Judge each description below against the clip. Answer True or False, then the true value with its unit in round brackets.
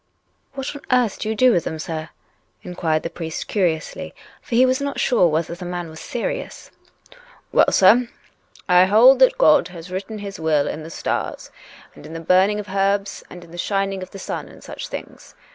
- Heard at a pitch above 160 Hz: True (190 Hz)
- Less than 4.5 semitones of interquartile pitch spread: False (5.1 semitones)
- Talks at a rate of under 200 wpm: False (205 wpm)